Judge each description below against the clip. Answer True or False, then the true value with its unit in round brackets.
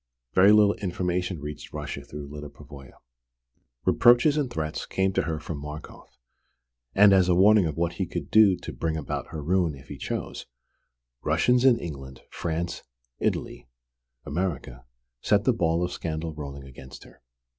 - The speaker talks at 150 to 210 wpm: True (160 wpm)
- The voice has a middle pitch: False (85 Hz)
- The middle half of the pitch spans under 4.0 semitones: False (4.4 semitones)